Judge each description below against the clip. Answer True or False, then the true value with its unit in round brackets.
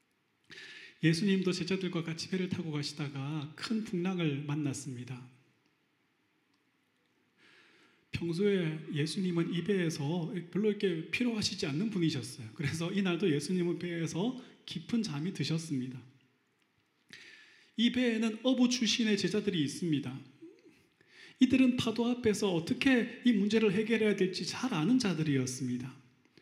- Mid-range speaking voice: True (180 Hz)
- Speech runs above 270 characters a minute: True (285 characters per minute)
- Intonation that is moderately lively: False (6.6 semitones)